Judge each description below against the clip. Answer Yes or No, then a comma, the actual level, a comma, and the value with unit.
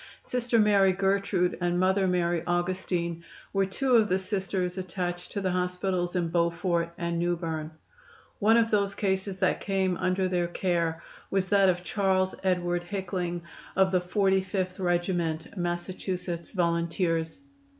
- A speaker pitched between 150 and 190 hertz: Yes, medium, 185 Hz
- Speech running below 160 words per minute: Yes, average, 140 wpm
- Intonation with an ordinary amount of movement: No, narrow, 1.8 semitones